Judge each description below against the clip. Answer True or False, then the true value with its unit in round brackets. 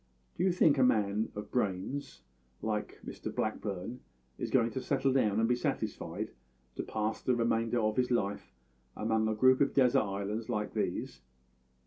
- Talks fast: False (170 wpm)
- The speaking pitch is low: True (115 Hz)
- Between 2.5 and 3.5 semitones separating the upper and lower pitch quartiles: True (3.2 semitones)